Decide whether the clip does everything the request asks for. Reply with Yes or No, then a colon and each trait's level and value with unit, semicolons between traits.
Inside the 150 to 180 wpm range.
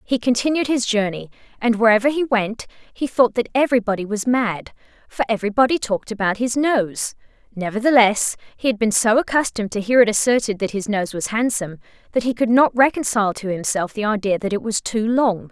No: average, 190 wpm